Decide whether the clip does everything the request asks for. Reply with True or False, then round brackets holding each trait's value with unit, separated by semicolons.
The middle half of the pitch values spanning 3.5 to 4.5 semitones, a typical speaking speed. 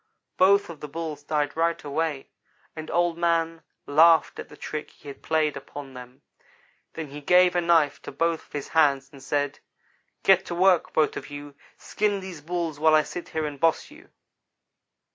False (2.8 semitones; 185 wpm)